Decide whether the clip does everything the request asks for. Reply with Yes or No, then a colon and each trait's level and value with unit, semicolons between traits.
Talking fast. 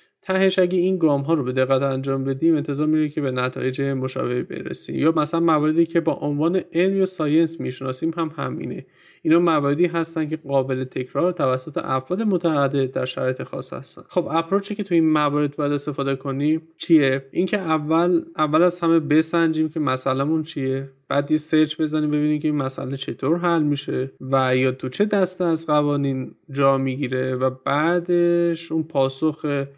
Yes: fast, 170 wpm